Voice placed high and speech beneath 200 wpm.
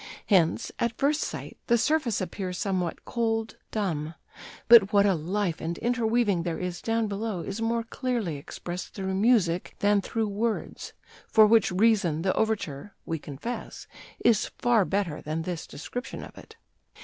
Yes: high, 205 Hz; average, 155 wpm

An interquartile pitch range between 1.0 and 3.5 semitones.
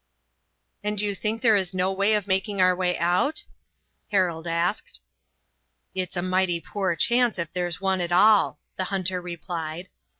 Yes: narrow, 2.4 semitones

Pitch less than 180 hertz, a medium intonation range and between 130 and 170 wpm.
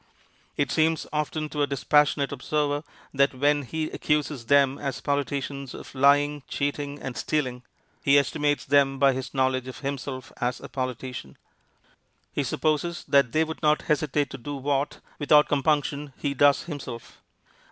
No: medium, 140 Hz; narrow, 1.8 semitones; average, 150 wpm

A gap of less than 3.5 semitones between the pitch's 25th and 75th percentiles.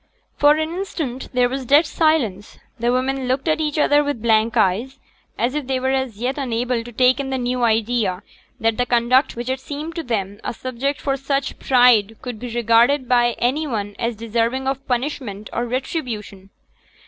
Yes: average, 2.9 semitones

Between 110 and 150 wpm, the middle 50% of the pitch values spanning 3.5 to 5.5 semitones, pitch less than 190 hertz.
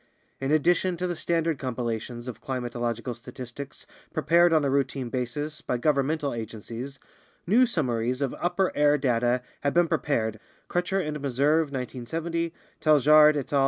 Yes: average, 145 wpm; average, 4.4 semitones; medium, 140 Hz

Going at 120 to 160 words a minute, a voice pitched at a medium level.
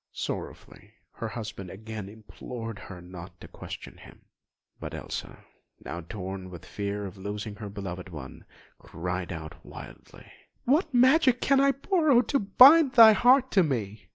No: average, 155 wpm; low, 110 Hz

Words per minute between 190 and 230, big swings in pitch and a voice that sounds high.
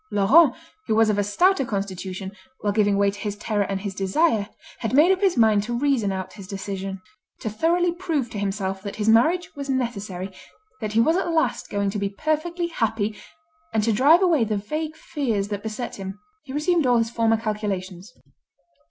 Yes: average, 195 wpm; wide, 6.2 semitones; high, 220 Hz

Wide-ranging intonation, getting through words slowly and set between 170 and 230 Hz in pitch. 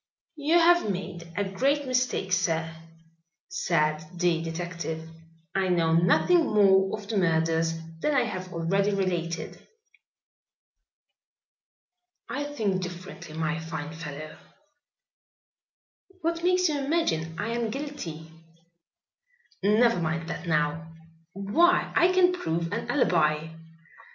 Yes: wide, 7.4 semitones; slow, 110 wpm; medium, 185 Hz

